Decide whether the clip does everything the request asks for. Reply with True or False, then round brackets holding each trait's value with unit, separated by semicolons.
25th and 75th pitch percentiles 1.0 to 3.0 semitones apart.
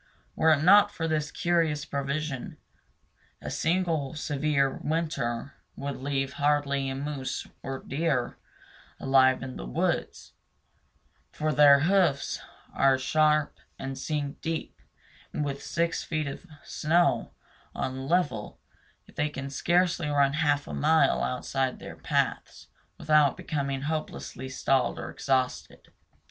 True (2.6 semitones)